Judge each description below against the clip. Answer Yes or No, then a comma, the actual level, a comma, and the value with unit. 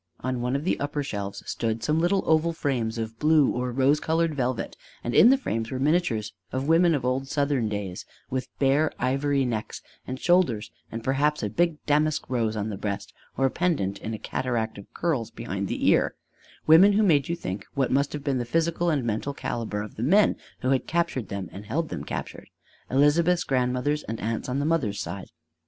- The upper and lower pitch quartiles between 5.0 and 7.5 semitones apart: Yes, wide, 5.5 semitones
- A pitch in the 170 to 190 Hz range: No, low, 130 Hz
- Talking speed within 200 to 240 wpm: Yes, fast, 205 wpm